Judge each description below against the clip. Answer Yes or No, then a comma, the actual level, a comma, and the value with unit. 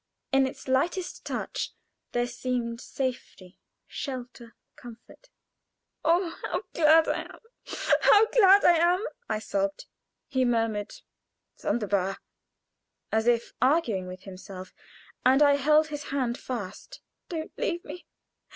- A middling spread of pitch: No, wide, 6.1 semitones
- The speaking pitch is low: No, very high, 255 Hz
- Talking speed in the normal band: No, slow, 120 wpm